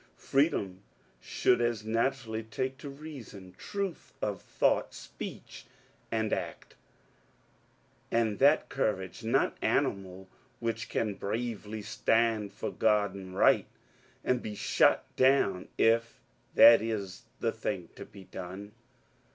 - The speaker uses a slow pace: Yes, slow, 120 wpm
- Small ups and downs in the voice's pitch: No, average, 3.4 semitones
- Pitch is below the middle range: Yes, low, 110 Hz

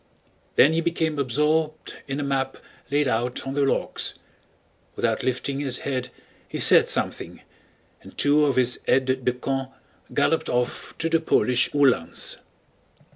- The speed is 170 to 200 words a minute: No, average, 145 wpm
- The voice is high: No, low, 135 Hz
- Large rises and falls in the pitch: No, narrow, 2.5 semitones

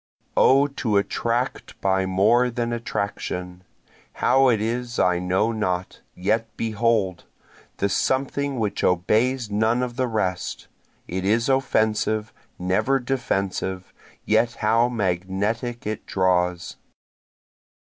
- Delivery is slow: Yes, slow, 110 wpm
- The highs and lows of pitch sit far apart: No, average, 4.2 semitones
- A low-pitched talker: Yes, low, 110 Hz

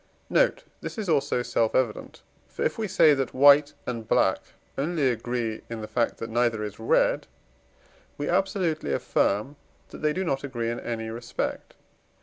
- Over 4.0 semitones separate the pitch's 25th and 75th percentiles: Yes, average, 4.6 semitones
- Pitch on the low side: Yes, low, 125 Hz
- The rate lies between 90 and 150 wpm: No, average, 165 wpm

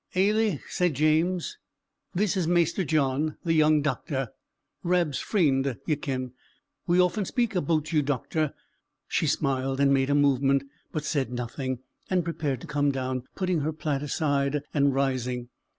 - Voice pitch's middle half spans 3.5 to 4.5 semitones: Yes, average, 4.0 semitones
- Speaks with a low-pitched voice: No, medium, 150 Hz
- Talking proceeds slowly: No, average, 150 wpm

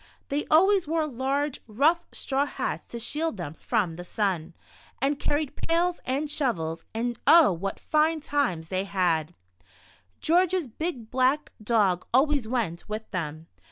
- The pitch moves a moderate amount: No, wide, 8.1 semitones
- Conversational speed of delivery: Yes, average, 160 wpm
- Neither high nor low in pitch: No, very high, 255 Hz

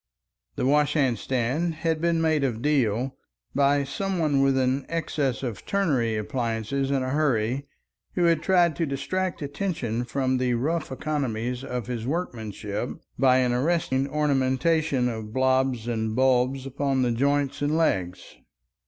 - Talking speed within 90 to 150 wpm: Yes, average, 145 wpm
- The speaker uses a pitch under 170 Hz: Yes, low, 135 Hz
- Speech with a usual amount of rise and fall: Yes, average, 3.6 semitones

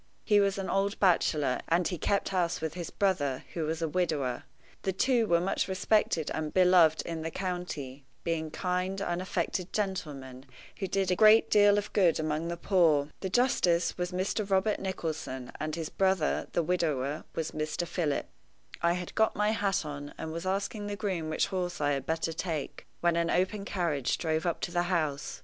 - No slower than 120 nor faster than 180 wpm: No, average, 190 wpm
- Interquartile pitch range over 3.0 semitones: Yes, average, 3.4 semitones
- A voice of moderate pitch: Yes, medium, 175 Hz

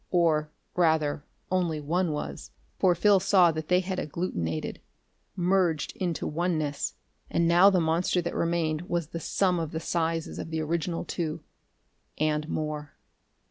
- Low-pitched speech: No, medium, 165 Hz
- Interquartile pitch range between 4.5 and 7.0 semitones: No, narrow, 2.4 semitones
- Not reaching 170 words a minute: Yes, average, 145 wpm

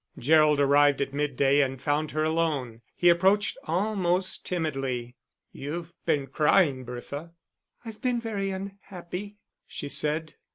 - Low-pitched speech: No, medium, 155 Hz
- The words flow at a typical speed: No, slow, 125 wpm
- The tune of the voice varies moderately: Yes, average, 4.7 semitones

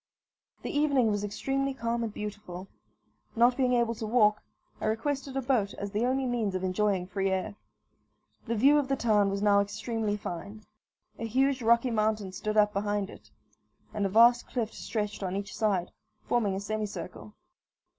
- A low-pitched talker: No, high, 215 Hz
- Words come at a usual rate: Yes, average, 175 wpm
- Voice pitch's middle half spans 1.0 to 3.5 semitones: Yes, average, 3.0 semitones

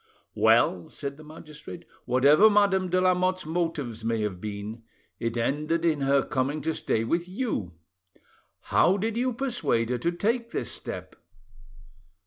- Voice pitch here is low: No, medium, 155 Hz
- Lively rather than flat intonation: Yes, wide, 7.6 semitones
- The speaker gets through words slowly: No, average, 145 wpm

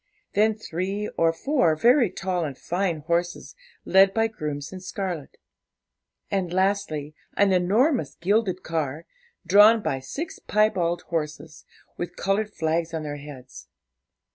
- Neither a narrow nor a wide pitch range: Yes, average, 4.3 semitones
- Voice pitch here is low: No, medium, 180 Hz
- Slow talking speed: Yes, slow, 130 wpm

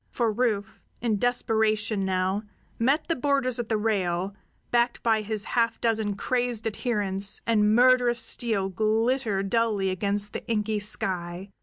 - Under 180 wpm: Yes, average, 140 wpm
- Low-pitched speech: No, high, 220 Hz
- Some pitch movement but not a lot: Yes, average, 3.0 semitones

